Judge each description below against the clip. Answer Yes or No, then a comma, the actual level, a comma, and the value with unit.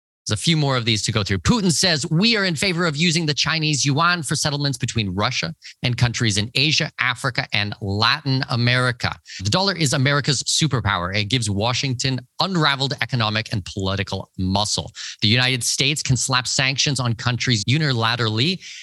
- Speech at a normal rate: Yes, average, 170 wpm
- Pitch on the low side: Yes, low, 130 Hz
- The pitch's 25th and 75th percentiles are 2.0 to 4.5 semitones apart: No, average, 5.2 semitones